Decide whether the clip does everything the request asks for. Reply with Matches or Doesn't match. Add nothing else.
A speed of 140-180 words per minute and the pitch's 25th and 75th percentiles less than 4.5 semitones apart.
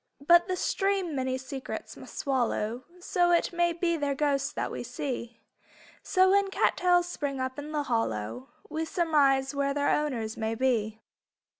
Doesn't match